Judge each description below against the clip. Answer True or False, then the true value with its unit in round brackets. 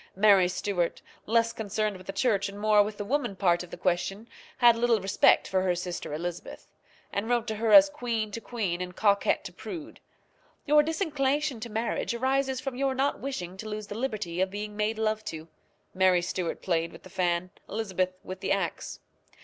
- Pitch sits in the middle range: False (210 Hz)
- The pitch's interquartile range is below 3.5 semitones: False (4.4 semitones)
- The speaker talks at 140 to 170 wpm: False (195 wpm)